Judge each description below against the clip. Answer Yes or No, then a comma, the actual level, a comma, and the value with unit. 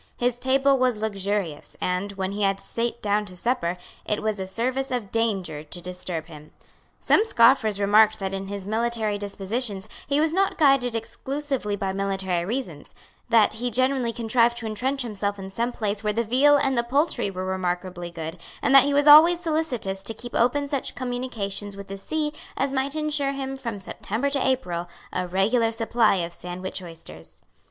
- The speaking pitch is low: No, high, 220 Hz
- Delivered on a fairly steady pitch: No, average, 5.2 semitones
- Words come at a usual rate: Yes, average, 180 wpm